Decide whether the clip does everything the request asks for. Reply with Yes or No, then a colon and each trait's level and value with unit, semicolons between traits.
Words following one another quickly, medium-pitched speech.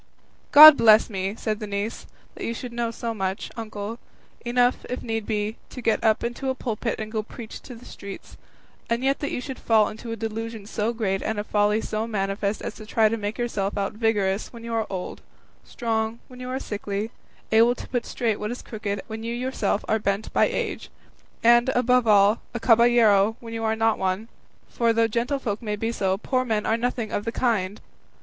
No: fast, 210 wpm; high, 225 Hz